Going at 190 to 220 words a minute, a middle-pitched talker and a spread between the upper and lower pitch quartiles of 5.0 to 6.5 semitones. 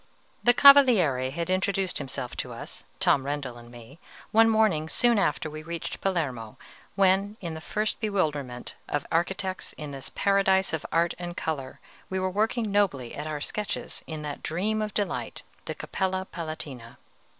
No: average, 160 wpm; medium, 170 Hz; average, 5.3 semitones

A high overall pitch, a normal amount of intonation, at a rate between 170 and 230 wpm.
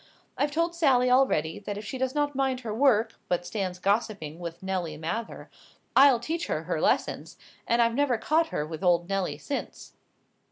No: high, 230 Hz; wide, 7.0 semitones; average, 185 wpm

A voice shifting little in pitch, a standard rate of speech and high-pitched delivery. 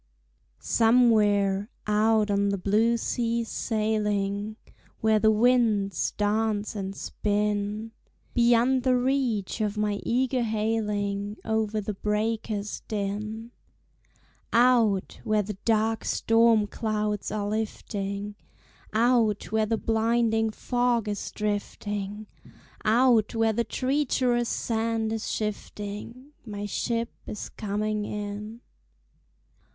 No: narrow, 1.8 semitones; slow, 105 wpm; high, 215 Hz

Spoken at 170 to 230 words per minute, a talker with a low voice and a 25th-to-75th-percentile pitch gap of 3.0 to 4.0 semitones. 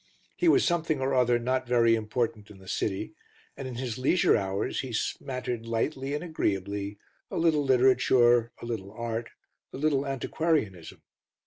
No: average, 155 wpm; low, 120 Hz; average, 3.6 semitones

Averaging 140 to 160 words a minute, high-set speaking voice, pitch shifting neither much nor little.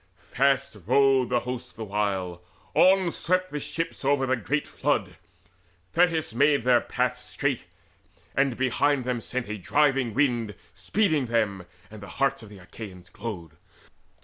No: average, 145 wpm; low, 125 Hz; average, 4.9 semitones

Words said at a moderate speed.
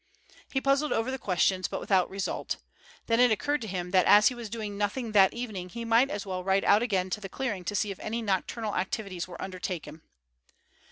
No: fast, 215 wpm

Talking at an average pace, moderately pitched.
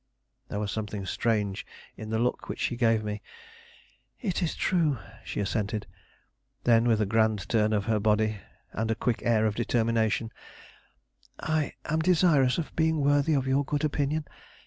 No: average, 165 wpm; low, 115 Hz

